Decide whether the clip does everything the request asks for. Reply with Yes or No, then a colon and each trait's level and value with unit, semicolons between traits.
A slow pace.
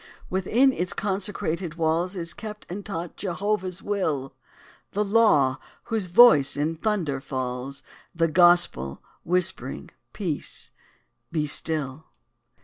Yes: slow, 110 wpm